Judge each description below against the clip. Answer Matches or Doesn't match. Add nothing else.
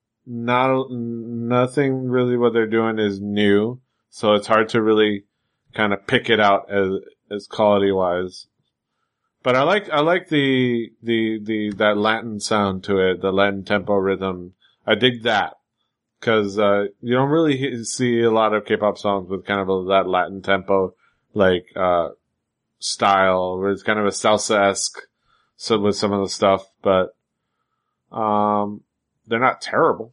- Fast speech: Doesn't match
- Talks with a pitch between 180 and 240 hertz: Doesn't match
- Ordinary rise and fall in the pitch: Matches